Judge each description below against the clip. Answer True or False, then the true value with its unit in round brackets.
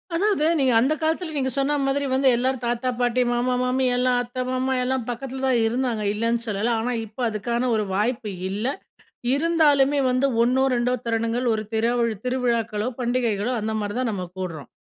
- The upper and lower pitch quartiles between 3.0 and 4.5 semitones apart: False (2.4 semitones)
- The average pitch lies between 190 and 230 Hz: False (245 Hz)